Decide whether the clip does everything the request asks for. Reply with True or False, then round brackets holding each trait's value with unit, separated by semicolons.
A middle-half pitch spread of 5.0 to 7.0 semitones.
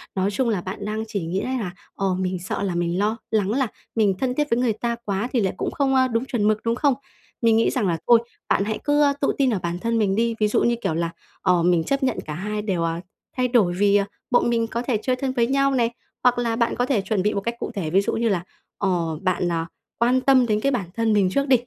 False (4.4 semitones)